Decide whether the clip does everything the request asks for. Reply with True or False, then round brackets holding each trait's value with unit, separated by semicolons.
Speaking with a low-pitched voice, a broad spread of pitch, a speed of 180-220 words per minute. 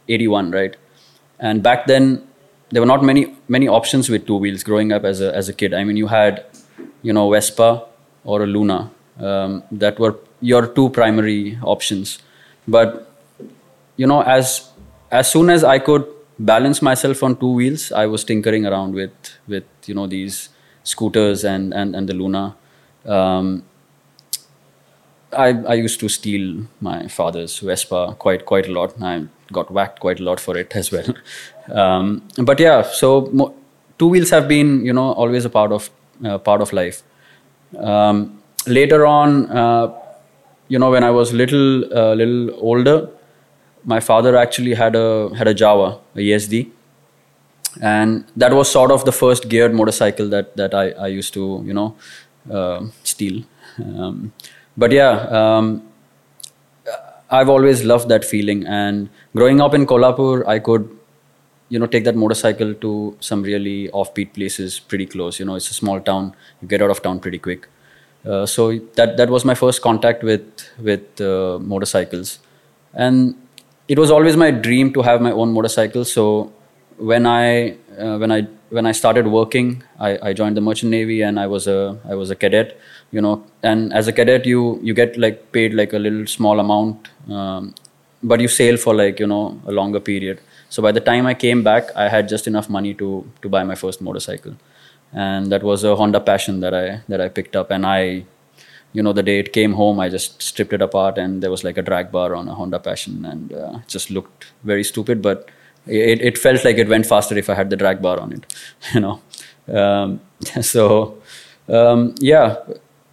False (110 Hz; 3.3 semitones; 185 wpm)